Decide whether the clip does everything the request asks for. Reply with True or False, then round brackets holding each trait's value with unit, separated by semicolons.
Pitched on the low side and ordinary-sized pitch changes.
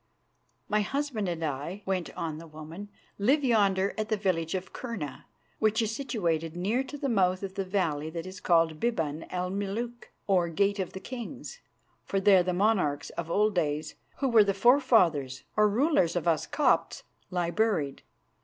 False (190 Hz; 4.6 semitones)